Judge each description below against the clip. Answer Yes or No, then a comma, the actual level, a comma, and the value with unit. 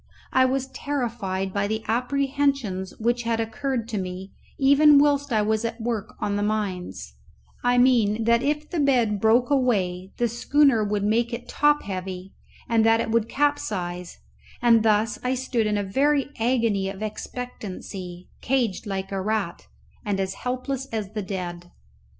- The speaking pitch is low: No, high, 225 Hz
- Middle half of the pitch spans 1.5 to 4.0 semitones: No, average, 4.4 semitones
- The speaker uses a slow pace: No, average, 160 wpm